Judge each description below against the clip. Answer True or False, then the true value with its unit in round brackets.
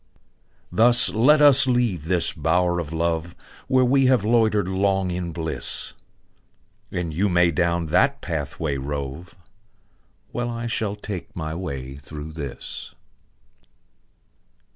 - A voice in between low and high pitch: False (90 Hz)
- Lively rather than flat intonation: True (5.8 semitones)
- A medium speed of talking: False (120 wpm)